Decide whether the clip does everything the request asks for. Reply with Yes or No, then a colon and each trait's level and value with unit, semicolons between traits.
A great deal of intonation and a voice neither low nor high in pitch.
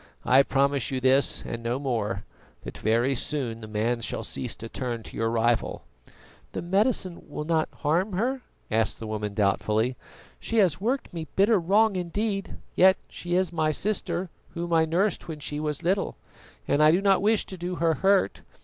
Yes: wide, 7.8 semitones; medium, 155 Hz